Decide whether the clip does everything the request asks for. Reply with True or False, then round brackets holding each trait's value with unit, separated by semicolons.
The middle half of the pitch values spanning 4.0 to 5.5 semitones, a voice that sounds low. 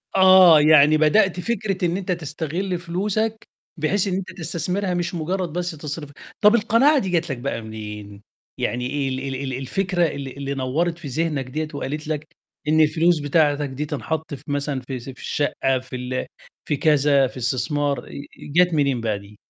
False (4.8 semitones; 155 Hz)